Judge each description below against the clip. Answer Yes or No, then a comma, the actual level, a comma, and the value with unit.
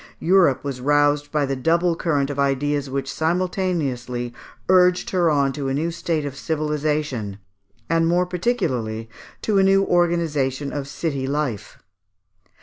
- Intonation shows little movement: No, average, 4.0 semitones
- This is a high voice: No, medium, 150 Hz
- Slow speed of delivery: No, average, 145 wpm